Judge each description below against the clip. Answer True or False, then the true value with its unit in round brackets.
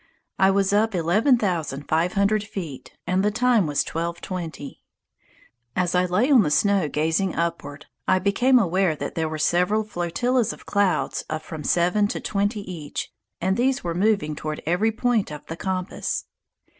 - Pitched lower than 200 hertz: True (185 Hz)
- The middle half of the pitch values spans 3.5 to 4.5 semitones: True (4.2 semitones)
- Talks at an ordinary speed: True (170 wpm)